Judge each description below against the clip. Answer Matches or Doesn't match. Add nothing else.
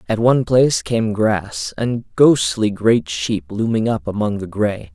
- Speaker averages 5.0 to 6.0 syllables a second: Doesn't match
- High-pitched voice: Doesn't match